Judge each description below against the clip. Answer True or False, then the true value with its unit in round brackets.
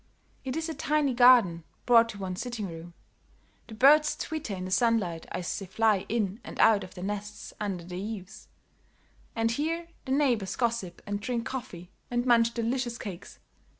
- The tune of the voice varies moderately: True (4.6 semitones)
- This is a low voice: False (225 Hz)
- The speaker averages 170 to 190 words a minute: True (175 wpm)